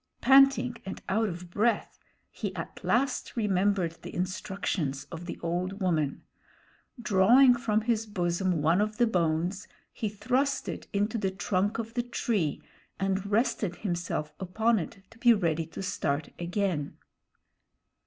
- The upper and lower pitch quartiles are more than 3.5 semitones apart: Yes, average, 4.5 semitones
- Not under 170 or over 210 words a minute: No, average, 145 wpm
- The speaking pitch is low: No, high, 195 Hz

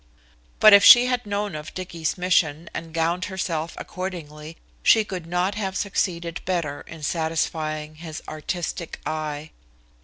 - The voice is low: No, medium, 170 Hz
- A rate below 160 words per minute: Yes, average, 140 wpm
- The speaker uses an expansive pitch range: No, average, 3.2 semitones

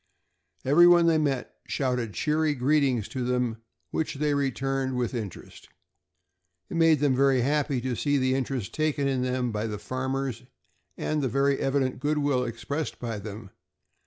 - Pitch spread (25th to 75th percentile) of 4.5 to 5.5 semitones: No, narrow, 2.6 semitones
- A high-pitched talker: No, low, 135 Hz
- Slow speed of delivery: No, average, 160 wpm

